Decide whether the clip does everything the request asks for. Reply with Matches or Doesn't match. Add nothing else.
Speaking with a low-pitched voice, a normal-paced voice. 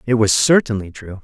Matches